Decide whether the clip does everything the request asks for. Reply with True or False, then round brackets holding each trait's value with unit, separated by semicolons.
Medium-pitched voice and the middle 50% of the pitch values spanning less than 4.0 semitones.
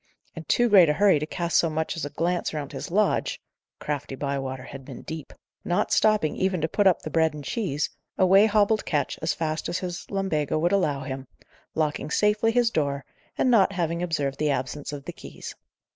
False (160 Hz; 4.8 semitones)